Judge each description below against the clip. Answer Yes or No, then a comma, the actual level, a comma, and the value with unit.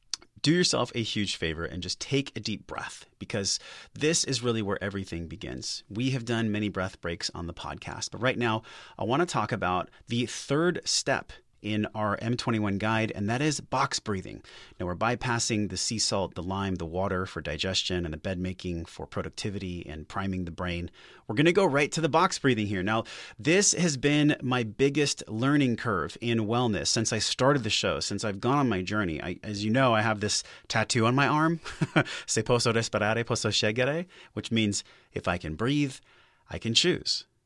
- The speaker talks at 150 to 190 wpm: No, average, 200 wpm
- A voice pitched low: Yes, low, 110 Hz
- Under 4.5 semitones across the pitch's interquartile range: No, average, 5.1 semitones